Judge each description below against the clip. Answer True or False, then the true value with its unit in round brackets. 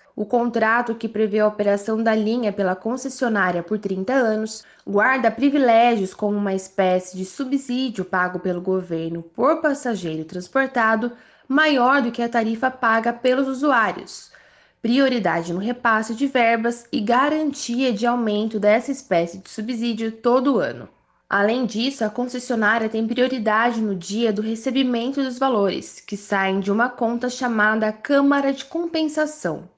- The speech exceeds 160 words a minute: False (140 wpm)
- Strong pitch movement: False (3.7 semitones)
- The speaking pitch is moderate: False (230 Hz)